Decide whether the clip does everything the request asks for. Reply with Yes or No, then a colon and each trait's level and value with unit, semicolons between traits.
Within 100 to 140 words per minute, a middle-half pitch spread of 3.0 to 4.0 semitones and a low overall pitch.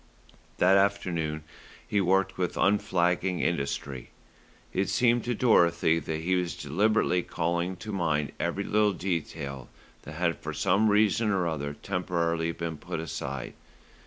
Yes: slow, 135 wpm; average, 3.6 semitones; very low, 85 Hz